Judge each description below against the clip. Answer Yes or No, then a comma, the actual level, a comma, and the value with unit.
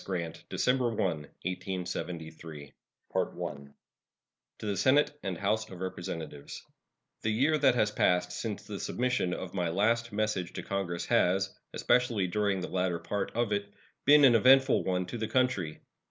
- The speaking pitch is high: No, low, 100 Hz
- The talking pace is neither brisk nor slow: Yes, average, 150 wpm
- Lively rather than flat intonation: No, average, 4.7 semitones